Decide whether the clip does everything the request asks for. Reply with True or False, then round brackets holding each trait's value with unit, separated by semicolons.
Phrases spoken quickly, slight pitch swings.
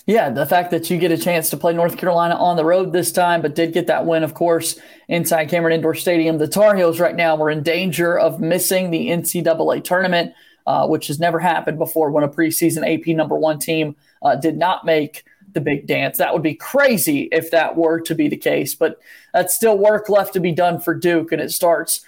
True (230 wpm; 1.8 semitones)